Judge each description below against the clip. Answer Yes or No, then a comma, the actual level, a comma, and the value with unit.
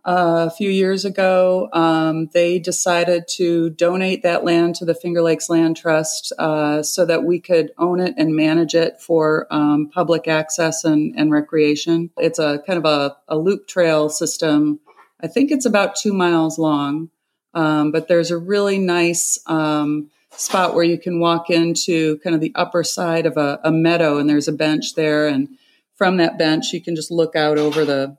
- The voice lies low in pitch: No, medium, 165 Hz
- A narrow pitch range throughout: Yes, narrow, 2.1 semitones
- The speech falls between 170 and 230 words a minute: Yes, average, 190 wpm